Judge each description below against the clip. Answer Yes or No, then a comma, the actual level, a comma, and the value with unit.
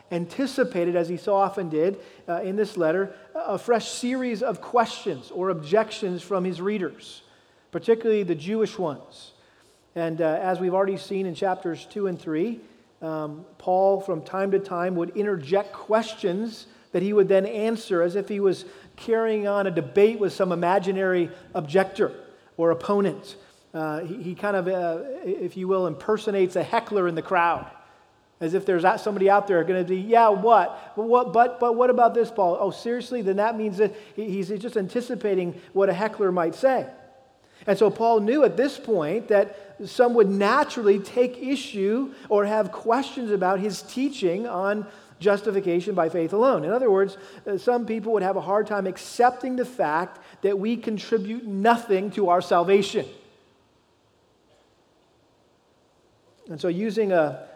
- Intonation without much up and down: No, average, 3.3 semitones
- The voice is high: Yes, high, 200 Hz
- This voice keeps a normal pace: Yes, average, 165 wpm